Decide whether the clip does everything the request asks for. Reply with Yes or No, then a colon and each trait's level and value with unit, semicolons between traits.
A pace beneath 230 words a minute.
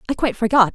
No: fast, 245 wpm